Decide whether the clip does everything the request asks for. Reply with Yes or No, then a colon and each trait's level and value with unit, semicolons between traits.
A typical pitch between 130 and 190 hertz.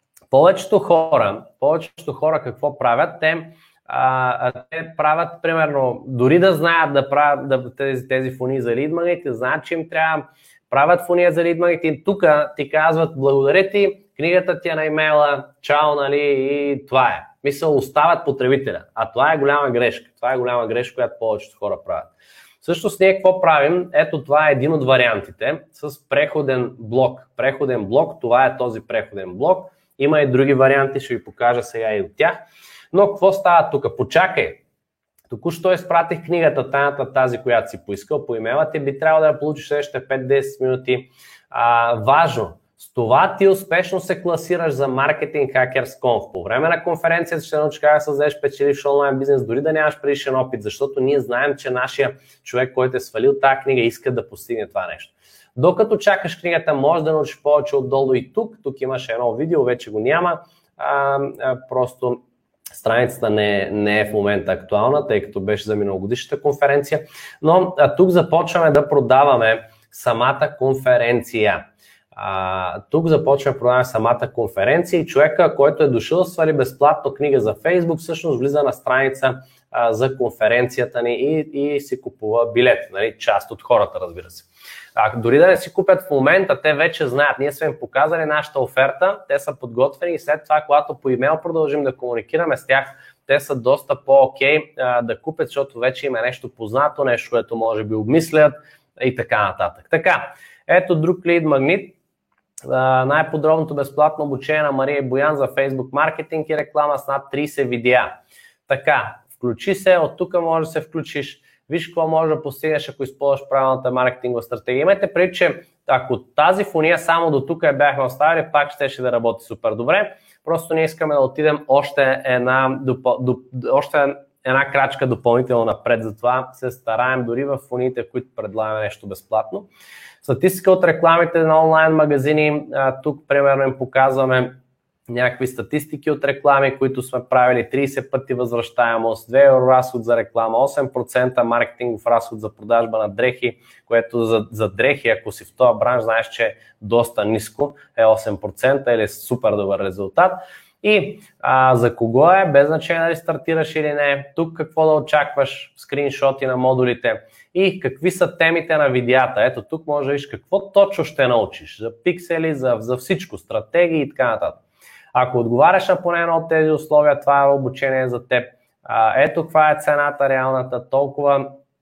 Yes: medium, 140 Hz